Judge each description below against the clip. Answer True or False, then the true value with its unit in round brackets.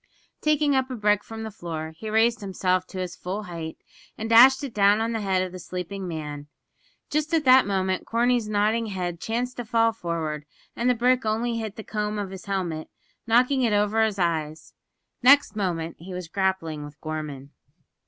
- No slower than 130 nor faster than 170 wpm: False (195 wpm)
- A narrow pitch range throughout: False (4.7 semitones)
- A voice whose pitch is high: True (205 Hz)